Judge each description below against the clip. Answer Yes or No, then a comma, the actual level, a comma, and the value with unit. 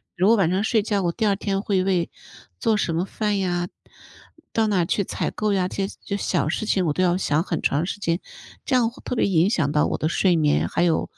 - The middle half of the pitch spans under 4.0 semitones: Yes, average, 3.3 semitones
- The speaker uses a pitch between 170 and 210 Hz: Yes, high, 190 Hz